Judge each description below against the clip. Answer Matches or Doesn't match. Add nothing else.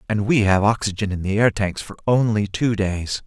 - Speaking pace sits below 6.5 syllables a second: Matches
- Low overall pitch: Matches